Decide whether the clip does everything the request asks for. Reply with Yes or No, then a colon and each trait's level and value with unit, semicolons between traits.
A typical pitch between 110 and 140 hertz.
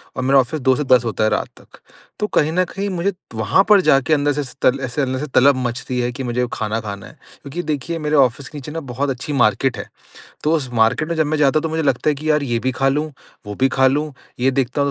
Yes: low, 135 Hz